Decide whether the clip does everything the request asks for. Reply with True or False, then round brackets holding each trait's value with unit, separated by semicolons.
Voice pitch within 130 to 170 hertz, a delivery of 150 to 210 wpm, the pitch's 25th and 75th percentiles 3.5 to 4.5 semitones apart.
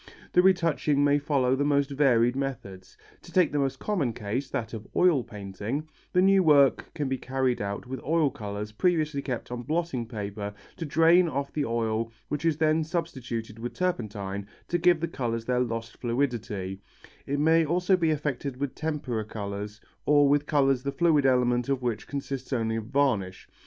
False (135 Hz; 180 wpm; 5.0 semitones)